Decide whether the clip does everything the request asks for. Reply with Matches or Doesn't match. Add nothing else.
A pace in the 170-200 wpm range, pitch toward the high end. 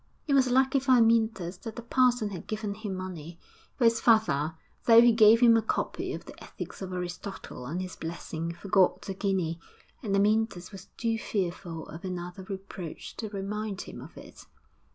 Matches